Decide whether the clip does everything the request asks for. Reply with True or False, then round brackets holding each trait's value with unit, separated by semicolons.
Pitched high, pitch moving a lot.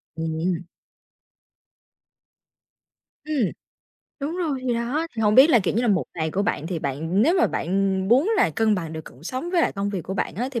True (205 Hz; 7.1 semitones)